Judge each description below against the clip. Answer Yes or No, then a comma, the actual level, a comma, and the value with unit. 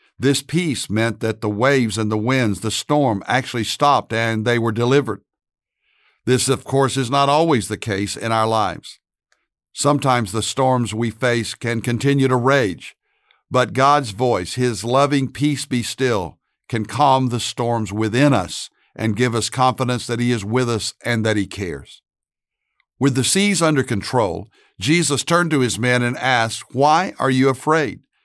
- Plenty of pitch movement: No, average, 3.2 semitones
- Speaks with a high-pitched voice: No, low, 125 Hz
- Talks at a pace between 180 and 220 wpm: No, average, 170 wpm